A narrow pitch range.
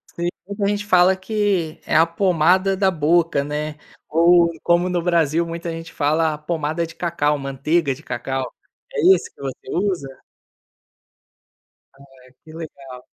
No: average, 3.1 semitones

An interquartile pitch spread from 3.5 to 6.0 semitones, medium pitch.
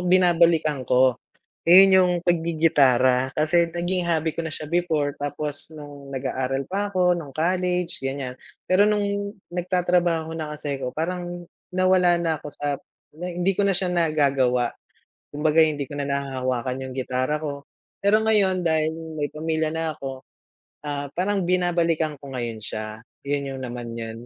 Yes: average, 4.2 semitones; medium, 155 Hz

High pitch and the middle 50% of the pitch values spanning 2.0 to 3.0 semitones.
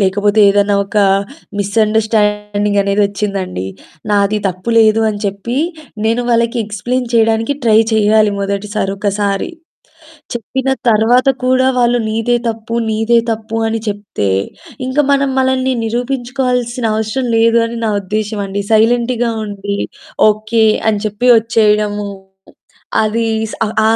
Yes: high, 220 Hz; narrow, 2.4 semitones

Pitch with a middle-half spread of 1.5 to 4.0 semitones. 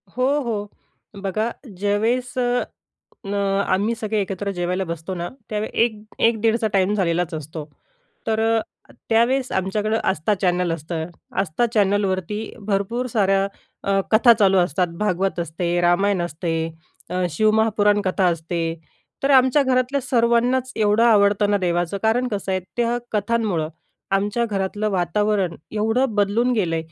Yes: average, 3.7 semitones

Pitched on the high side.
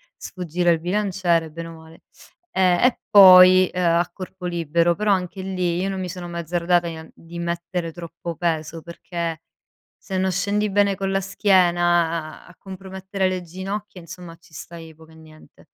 No: medium, 175 Hz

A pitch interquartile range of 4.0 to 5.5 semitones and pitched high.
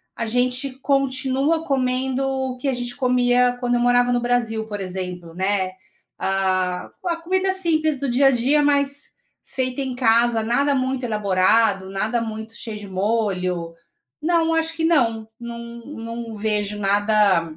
Yes: average, 4.3 semitones; high, 240 Hz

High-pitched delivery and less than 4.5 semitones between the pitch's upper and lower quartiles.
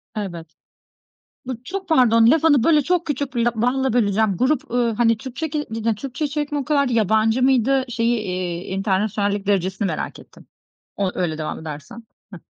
No: high, 230 Hz; average, 5.0 semitones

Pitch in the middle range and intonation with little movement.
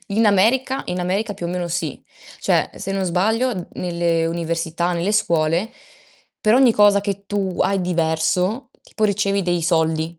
No: medium, 180 Hz; average, 3.3 semitones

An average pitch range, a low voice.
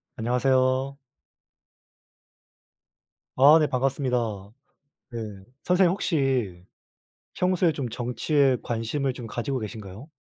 Yes: average, 3.2 semitones; low, 130 Hz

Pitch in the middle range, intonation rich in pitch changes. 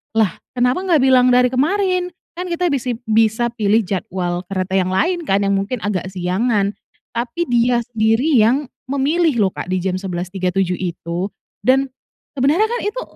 No: high, 235 Hz; wide, 6.3 semitones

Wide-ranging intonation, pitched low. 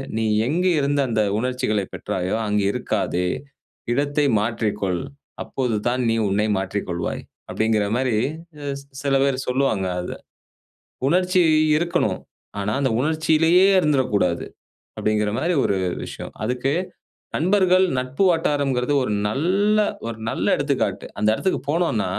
Yes: wide, 6.6 semitones; low, 130 Hz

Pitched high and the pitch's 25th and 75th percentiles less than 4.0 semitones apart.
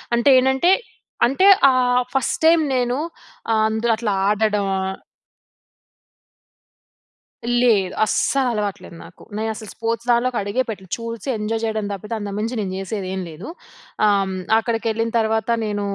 Yes: high, 220 Hz; average, 2.7 semitones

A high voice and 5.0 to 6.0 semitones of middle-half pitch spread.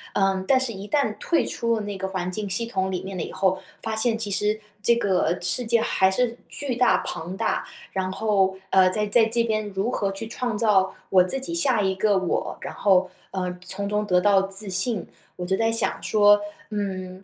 No: high, 200 Hz; average, 3.0 semitones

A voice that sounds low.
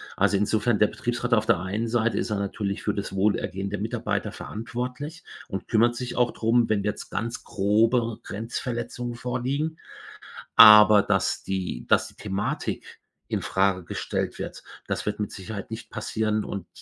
Yes: low, 110 Hz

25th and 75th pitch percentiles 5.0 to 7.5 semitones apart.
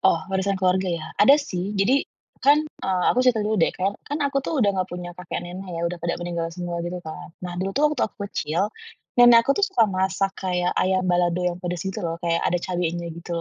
No: average, 3.2 semitones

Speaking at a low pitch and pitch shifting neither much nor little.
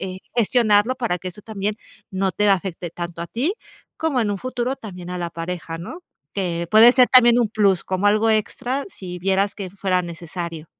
No: high, 195 Hz; average, 4.4 semitones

